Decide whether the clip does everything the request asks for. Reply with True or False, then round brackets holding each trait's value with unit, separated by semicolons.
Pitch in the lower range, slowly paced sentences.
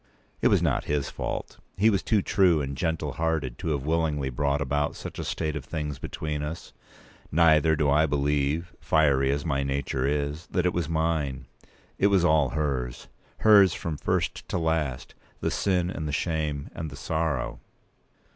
False (75 Hz; 165 wpm)